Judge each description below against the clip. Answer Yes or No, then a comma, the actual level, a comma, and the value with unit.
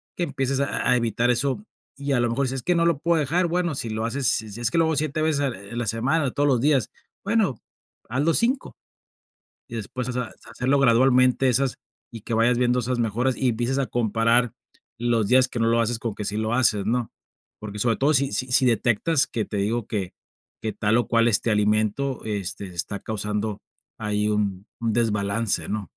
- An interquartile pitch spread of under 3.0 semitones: No, average, 3.8 semitones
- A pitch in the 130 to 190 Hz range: No, low, 120 Hz